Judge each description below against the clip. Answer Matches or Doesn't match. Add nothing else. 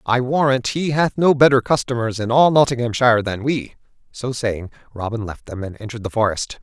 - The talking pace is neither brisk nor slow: Matches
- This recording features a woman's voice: Doesn't match